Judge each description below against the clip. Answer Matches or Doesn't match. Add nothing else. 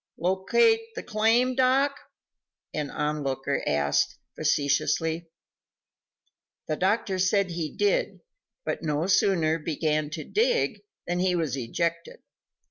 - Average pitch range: Doesn't match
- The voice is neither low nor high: Matches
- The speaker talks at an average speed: Doesn't match